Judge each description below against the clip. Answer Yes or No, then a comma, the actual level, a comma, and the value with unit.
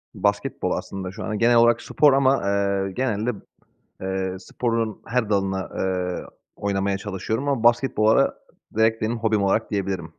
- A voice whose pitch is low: Yes, low, 105 Hz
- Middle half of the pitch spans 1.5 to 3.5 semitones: Yes, average, 3.2 semitones